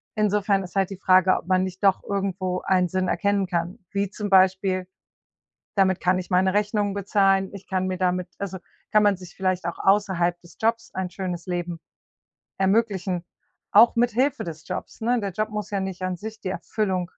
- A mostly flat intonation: Yes, narrow, 1.8 semitones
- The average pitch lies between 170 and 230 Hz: Yes, high, 190 Hz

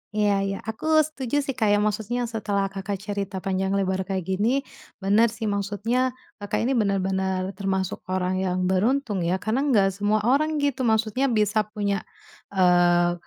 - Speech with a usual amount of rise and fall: Yes, average, 3.3 semitones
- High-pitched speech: Yes, high, 205 Hz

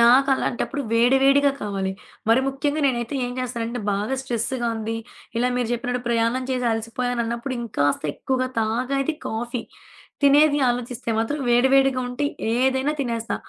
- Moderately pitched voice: No, high, 245 Hz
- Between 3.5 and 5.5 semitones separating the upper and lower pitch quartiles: No, narrow, 2.5 semitones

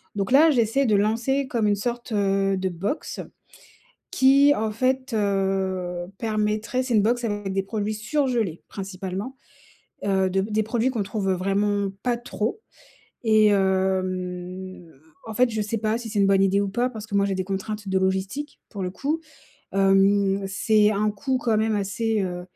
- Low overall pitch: No, high, 205 Hz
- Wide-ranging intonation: No, average, 3.0 semitones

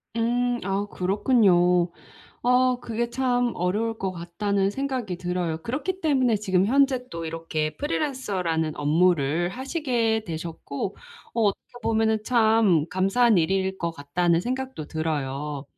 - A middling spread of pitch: No, wide, 6.2 semitones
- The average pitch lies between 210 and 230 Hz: No, high, 195 Hz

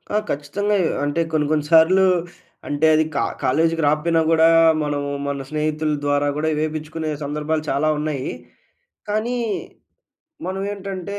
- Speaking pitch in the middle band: Yes, medium, 155 Hz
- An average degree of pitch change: No, narrow, 2.1 semitones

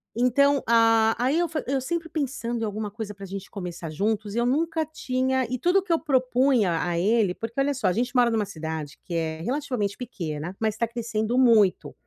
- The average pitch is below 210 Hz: No, high, 230 Hz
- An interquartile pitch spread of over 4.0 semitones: Yes, average, 4.6 semitones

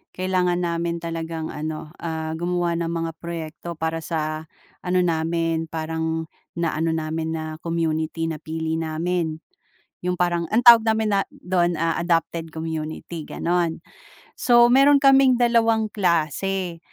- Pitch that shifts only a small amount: Yes, narrow, 1.9 semitones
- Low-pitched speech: No, medium, 165 Hz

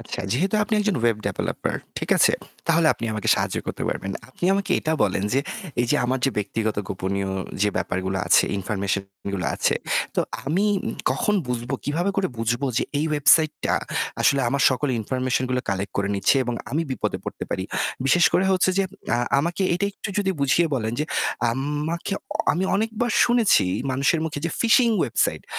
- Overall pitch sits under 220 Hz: Yes, medium, 140 Hz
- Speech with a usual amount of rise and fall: No, wide, 7.9 semitones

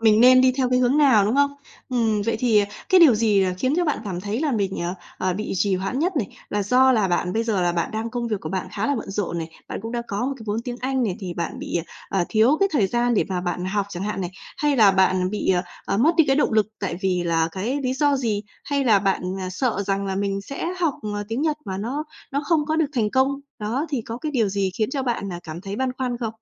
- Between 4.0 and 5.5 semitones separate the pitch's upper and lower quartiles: Yes, average, 5.2 semitones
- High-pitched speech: Yes, high, 220 Hz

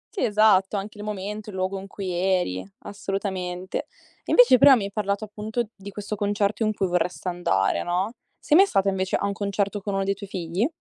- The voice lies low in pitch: No, high, 200 Hz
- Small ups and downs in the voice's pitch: Yes, narrow, 1.9 semitones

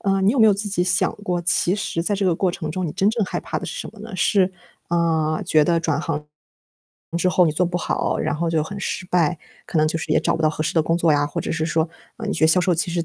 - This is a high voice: No, medium, 175 Hz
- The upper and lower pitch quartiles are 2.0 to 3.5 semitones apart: Yes, average, 3.0 semitones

